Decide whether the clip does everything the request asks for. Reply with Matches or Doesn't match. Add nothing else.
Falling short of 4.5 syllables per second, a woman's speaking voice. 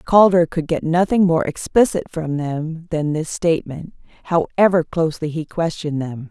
Doesn't match